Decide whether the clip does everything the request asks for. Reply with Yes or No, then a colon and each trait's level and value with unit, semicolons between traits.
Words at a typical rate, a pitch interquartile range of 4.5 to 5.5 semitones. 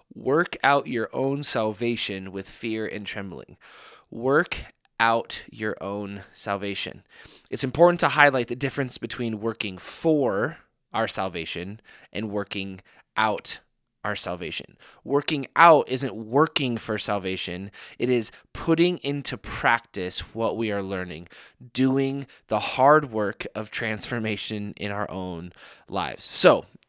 No: slow, 125 wpm; average, 5.1 semitones